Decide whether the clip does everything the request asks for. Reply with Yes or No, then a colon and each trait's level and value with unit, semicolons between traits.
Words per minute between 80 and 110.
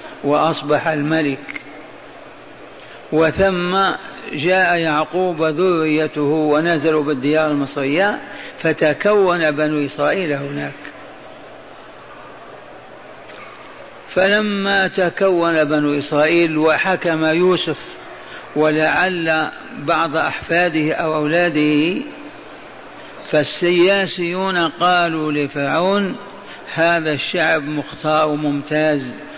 No: slow, 65 wpm